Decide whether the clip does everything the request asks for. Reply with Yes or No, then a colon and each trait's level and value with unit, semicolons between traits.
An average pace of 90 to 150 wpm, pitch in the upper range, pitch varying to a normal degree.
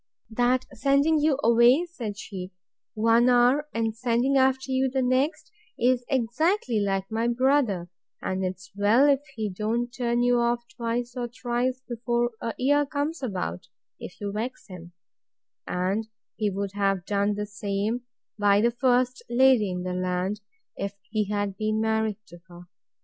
No: average, 160 wpm; high, 235 Hz; average, 3.9 semitones